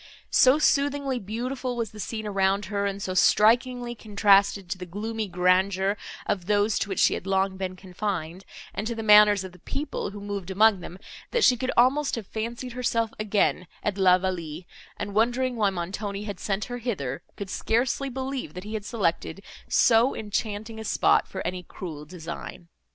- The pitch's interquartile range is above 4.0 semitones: No, average, 3.6 semitones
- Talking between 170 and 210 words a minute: Yes, average, 185 wpm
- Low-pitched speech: No, high, 205 Hz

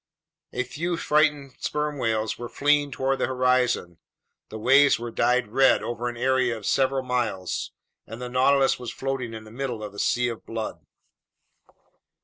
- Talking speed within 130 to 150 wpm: No, average, 165 wpm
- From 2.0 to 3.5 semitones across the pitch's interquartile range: Yes, average, 2.8 semitones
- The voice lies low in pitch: Yes, low, 125 Hz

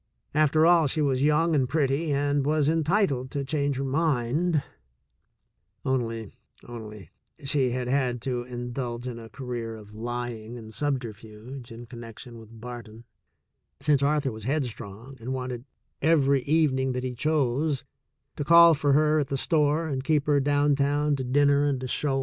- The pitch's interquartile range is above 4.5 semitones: No, average, 3.4 semitones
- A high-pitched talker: No, low, 135 Hz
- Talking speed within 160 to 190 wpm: Yes, average, 175 wpm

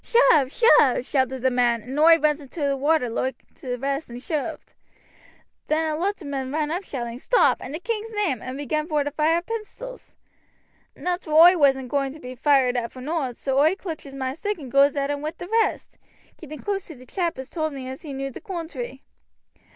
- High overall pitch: Yes, very high, 290 Hz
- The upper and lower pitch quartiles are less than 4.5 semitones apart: Yes, average, 3.9 semitones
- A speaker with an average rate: No, fast, 215 wpm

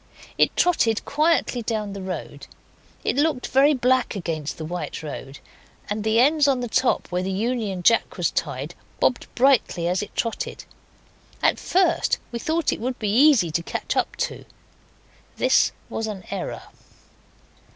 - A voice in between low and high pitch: No, high, 225 Hz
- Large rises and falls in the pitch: Yes, wide, 6.1 semitones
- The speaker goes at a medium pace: Yes, average, 160 wpm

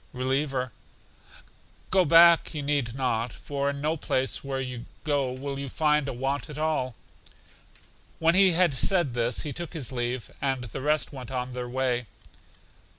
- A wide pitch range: No, average, 3.1 semitones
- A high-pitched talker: No, low, 135 Hz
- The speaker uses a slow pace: No, average, 165 wpm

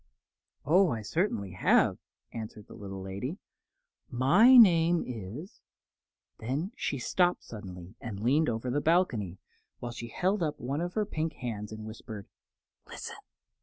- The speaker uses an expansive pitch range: Yes, wide, 7.8 semitones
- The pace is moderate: Yes, average, 145 wpm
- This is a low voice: Yes, low, 125 Hz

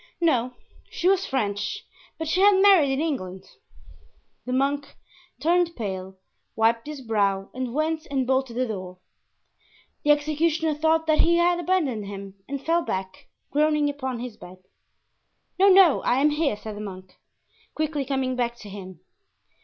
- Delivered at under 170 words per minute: Yes, average, 155 wpm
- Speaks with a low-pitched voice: No, very high, 270 Hz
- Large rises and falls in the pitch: Yes, wide, 6.6 semitones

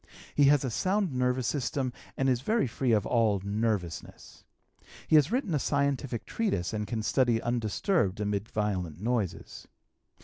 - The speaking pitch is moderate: No, low, 120 Hz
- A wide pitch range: No, average, 5.0 semitones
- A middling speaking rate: Yes, average, 150 wpm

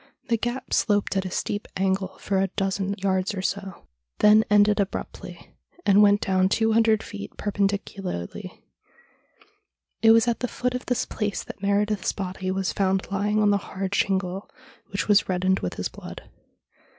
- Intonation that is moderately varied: No, narrow, 1.7 semitones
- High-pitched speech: Yes, high, 200 Hz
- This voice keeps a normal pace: Yes, average, 165 wpm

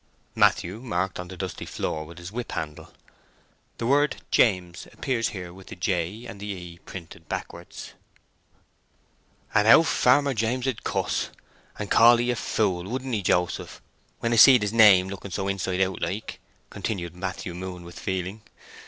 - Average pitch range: Yes, average, 4.4 semitones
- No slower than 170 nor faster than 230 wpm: Yes, average, 180 wpm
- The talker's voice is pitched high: No, very low, 95 Hz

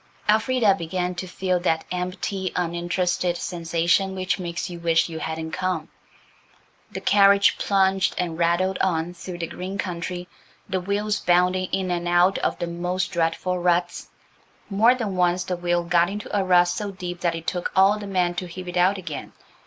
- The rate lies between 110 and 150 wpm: No, average, 175 wpm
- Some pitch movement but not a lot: No, narrow, 1.7 semitones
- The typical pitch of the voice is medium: Yes, medium, 180 Hz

